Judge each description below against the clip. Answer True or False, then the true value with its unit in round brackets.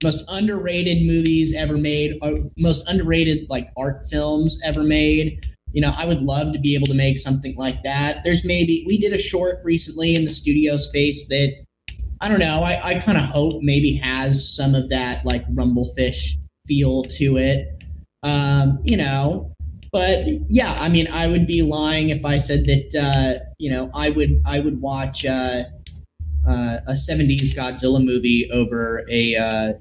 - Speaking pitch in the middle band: True (145 Hz)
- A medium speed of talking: True (175 wpm)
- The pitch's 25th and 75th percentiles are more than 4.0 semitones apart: False (3.3 semitones)